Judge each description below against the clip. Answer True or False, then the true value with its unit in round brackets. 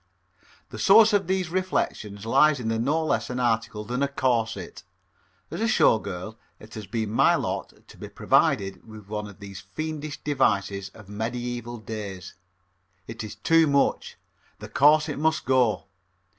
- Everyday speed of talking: True (155 wpm)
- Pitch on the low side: True (120 Hz)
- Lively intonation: True (5.9 semitones)